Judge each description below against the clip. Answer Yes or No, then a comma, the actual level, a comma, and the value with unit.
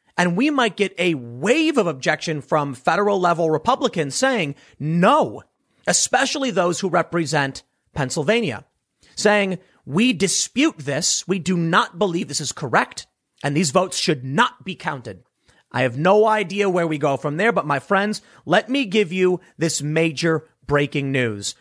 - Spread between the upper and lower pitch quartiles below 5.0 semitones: No, wide, 5.4 semitones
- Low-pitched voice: No, medium, 175 Hz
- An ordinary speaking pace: Yes, average, 160 wpm